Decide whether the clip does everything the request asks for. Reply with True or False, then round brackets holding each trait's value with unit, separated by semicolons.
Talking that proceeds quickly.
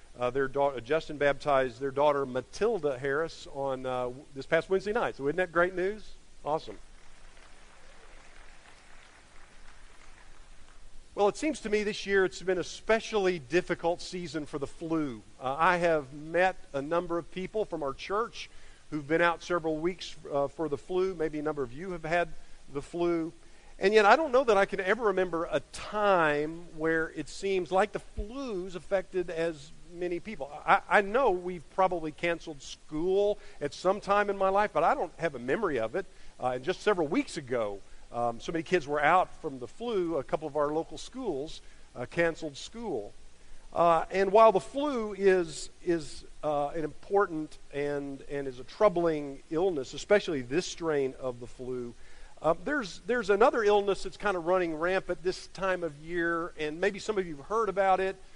False (185 wpm)